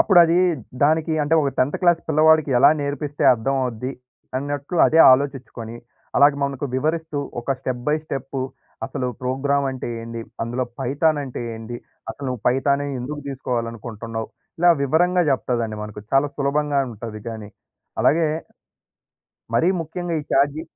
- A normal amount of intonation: Yes, average, 3.7 semitones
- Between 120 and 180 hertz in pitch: Yes, medium, 140 Hz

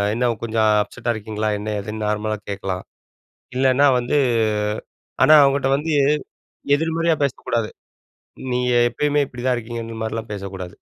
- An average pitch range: Yes, average, 3.9 semitones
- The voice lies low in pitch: Yes, low, 115 Hz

